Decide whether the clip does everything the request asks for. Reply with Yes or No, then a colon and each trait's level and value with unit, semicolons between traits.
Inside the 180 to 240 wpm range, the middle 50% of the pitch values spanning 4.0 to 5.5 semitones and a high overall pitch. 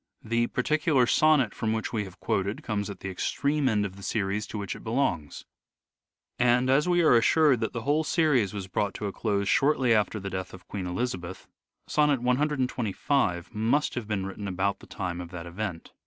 No: average, 200 wpm; average, 5.1 semitones; low, 110 Hz